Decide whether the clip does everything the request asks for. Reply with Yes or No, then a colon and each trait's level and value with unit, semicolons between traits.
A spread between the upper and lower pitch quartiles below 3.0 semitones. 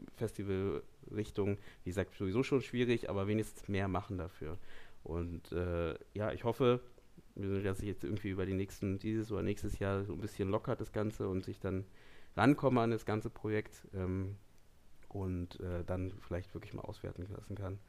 Yes: narrow, 2.5 semitones